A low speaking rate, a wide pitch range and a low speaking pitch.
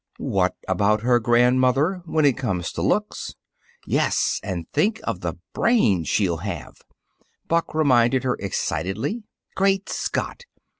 Yes: slow, 130 wpm; wide, 8.3 semitones; low, 120 Hz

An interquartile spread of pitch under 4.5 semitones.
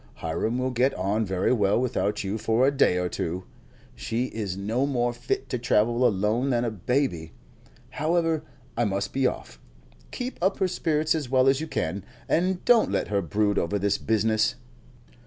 No: average, 5.1 semitones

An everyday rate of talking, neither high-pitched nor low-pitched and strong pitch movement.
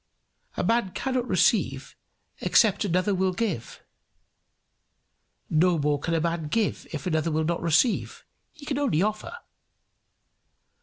No: slow, 130 wpm; medium, 180 Hz; wide, 5.8 semitones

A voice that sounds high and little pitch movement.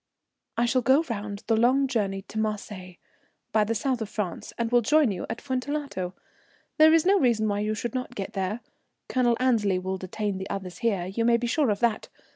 No: high, 220 Hz; average, 3.9 semitones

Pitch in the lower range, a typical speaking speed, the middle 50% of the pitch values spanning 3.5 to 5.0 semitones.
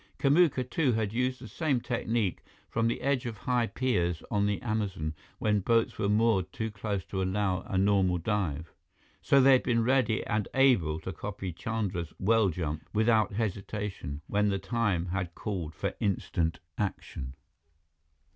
Yes: low, 105 Hz; average, 160 wpm; average, 3.9 semitones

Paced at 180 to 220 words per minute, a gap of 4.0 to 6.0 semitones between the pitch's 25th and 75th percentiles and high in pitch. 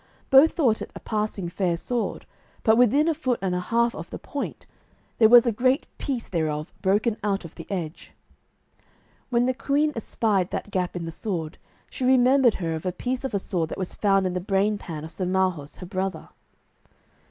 Yes: average, 200 wpm; average, 5.3 semitones; high, 200 Hz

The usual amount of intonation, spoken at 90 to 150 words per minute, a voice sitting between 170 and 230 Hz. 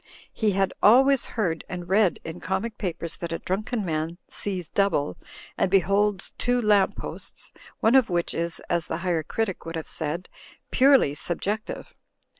No: average, 4.0 semitones; average, 160 wpm; high, 190 Hz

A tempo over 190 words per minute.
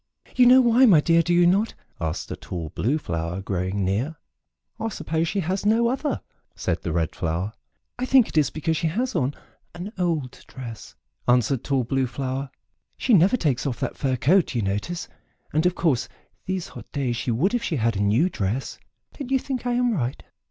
Yes: average, 200 wpm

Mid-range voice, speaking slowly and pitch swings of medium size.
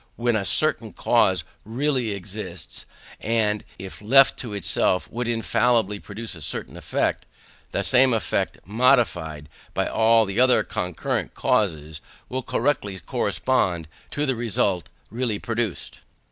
No: low, 110 Hz; slow, 130 wpm; average, 4.3 semitones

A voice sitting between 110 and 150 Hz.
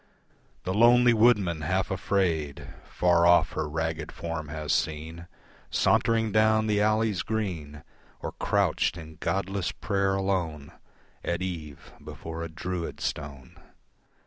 No: very low, 85 Hz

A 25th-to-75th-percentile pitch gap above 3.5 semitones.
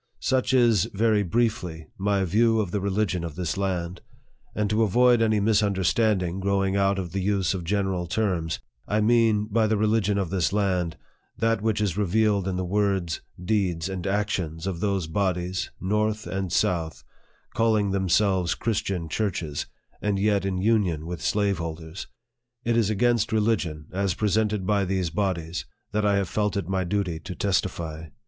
No: average, 3.0 semitones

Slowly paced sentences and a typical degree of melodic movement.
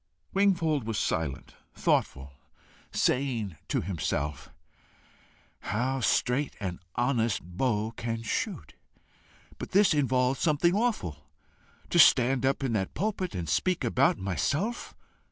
No: slow, 115 wpm; wide, 7.3 semitones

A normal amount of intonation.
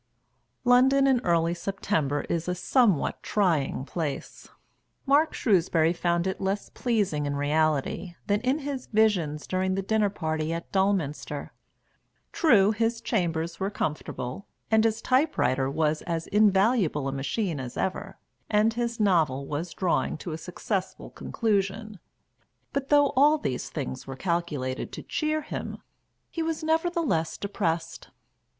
No: wide, 6.2 semitones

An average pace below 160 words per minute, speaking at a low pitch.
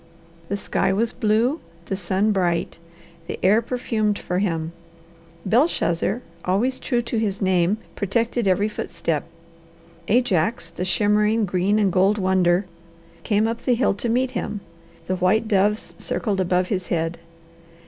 No: average, 140 wpm; high, 205 Hz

